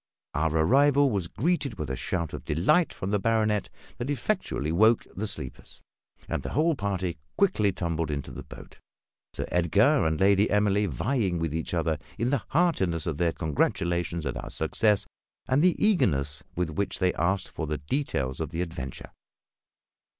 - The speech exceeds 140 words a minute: Yes, average, 165 wpm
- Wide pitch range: Yes, wide, 5.9 semitones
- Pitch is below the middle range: Yes, very low, 90 Hz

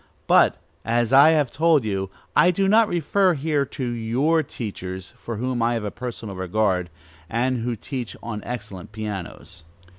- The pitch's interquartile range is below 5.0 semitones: No, wide, 5.4 semitones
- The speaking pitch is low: Yes, low, 120 Hz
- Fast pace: No, average, 160 wpm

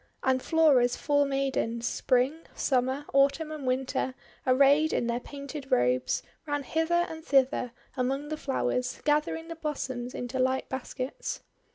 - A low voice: No, very high, 270 Hz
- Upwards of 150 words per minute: No, average, 140 wpm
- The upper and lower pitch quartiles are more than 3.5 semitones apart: No, average, 2.7 semitones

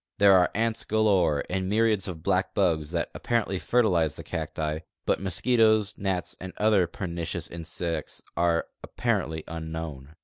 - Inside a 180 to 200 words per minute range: No, average, 140 wpm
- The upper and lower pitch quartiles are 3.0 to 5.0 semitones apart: Yes, average, 4.0 semitones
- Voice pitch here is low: Yes, very low, 90 Hz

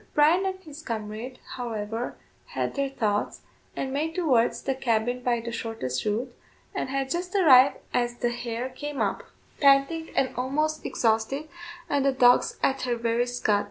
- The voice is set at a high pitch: Yes, very high, 255 Hz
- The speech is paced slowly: No, average, 160 wpm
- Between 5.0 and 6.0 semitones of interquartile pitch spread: No, average, 3.3 semitones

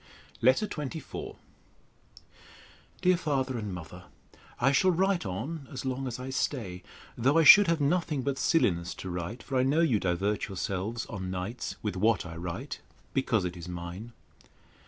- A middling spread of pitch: No, wide, 7.3 semitones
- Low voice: Yes, low, 120 Hz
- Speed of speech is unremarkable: Yes, average, 160 wpm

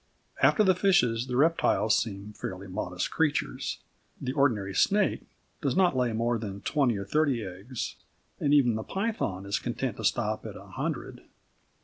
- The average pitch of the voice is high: No, low, 120 Hz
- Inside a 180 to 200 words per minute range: No, average, 160 wpm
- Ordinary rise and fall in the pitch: No, wide, 6.2 semitones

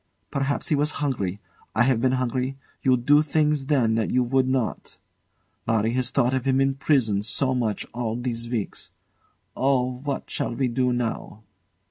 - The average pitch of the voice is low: Yes, low, 130 Hz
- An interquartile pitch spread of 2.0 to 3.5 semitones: Yes, narrow, 2.5 semitones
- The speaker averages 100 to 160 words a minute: No, average, 170 wpm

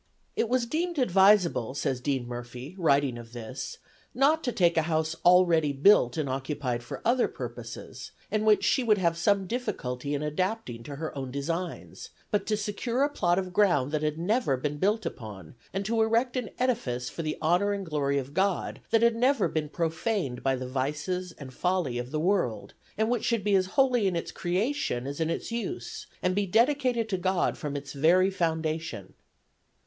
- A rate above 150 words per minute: Yes, average, 190 wpm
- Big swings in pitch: Yes, wide, 7.2 semitones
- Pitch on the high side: No, medium, 175 Hz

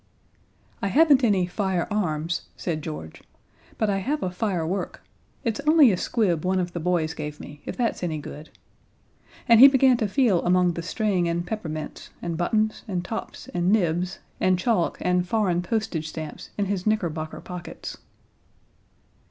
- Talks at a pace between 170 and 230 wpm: No, average, 160 wpm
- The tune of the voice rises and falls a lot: No, average, 4.2 semitones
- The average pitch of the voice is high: No, medium, 180 Hz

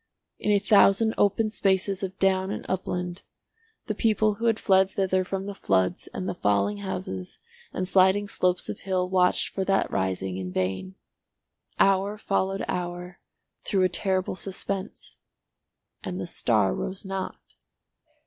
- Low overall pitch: No, high, 190 Hz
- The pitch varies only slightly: Yes, narrow, 2.0 semitones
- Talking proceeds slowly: No, average, 150 wpm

